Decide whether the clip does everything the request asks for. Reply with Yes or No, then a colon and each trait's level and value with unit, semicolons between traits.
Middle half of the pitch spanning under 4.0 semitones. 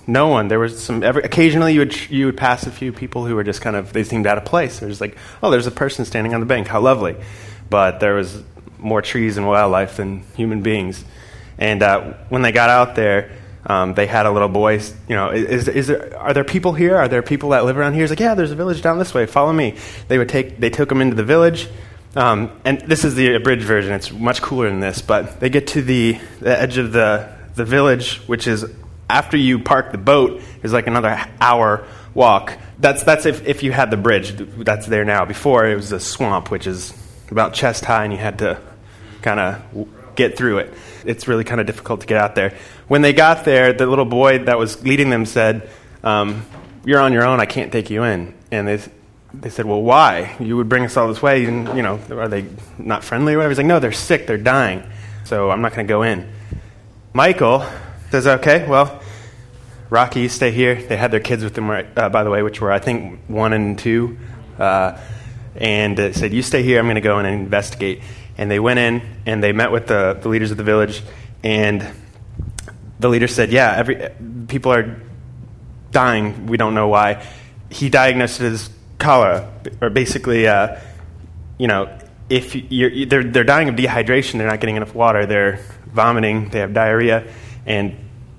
Yes: average, 3.2 semitones